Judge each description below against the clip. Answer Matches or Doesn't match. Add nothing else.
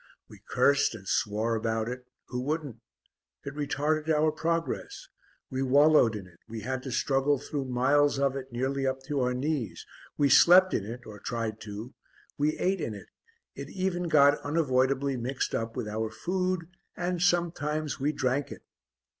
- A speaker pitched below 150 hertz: Matches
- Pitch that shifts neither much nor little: Matches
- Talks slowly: Doesn't match